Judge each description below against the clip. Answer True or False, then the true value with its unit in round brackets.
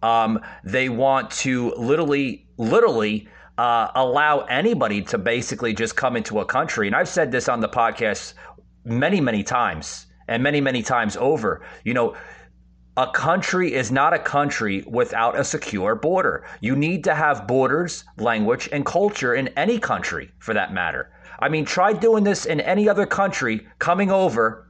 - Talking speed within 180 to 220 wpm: False (165 wpm)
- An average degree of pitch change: False (7.2 semitones)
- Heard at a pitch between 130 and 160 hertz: True (135 Hz)